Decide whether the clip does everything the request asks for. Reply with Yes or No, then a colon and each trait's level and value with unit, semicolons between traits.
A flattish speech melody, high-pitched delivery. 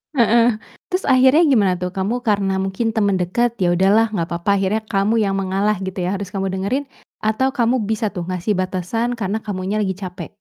No: average, 3.3 semitones; high, 200 Hz